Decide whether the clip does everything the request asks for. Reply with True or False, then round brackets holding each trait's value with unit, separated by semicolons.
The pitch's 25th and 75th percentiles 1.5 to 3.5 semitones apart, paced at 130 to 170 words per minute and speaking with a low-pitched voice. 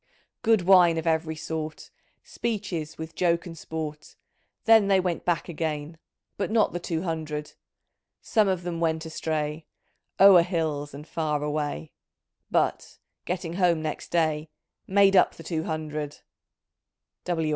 False (2.5 semitones; 145 wpm; 165 Hz)